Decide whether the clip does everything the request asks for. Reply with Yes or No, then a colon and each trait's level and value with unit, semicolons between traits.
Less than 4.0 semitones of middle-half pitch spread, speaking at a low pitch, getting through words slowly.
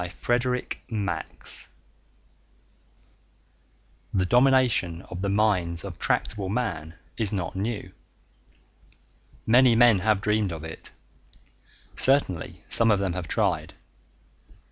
No: average, 4.5 semitones; low, 100 Hz; slow, 100 wpm